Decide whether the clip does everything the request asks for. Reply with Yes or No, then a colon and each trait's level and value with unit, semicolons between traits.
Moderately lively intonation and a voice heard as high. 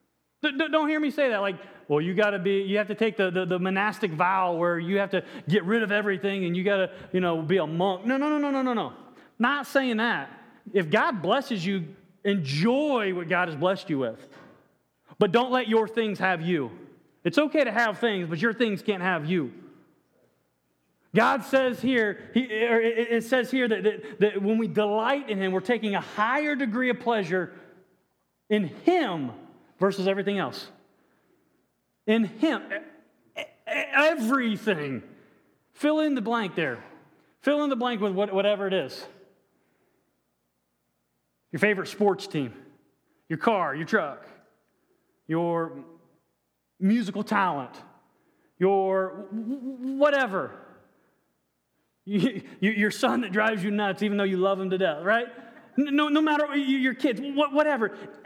Yes: average, 5.0 semitones; high, 210 Hz